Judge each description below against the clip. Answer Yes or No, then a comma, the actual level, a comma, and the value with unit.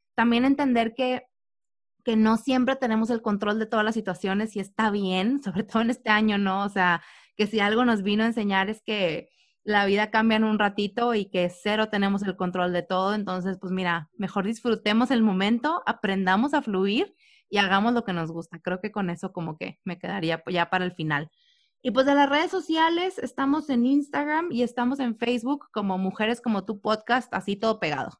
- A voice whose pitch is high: Yes, high, 215 Hz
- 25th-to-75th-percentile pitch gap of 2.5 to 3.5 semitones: No, average, 4.2 semitones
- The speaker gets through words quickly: Yes, fast, 205 wpm